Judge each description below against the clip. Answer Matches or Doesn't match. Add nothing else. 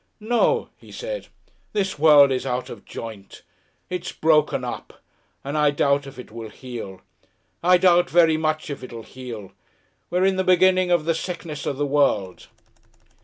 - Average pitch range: Doesn't match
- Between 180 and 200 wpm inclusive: Doesn't match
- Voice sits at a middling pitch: Matches